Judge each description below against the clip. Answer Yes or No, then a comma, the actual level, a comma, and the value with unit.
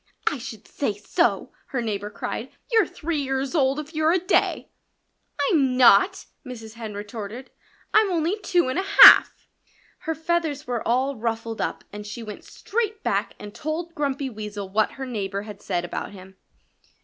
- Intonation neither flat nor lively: No, wide, 6.9 semitones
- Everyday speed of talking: Yes, average, 170 wpm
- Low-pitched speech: No, very high, 260 Hz